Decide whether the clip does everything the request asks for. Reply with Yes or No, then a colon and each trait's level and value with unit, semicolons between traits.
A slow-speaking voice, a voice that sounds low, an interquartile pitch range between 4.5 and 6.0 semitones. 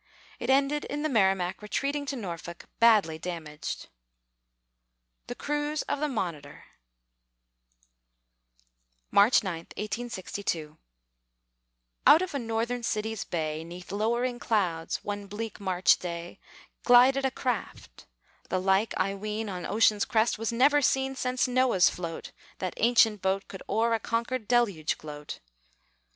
No: slow, 130 wpm; high, 215 Hz; average, 5.2 semitones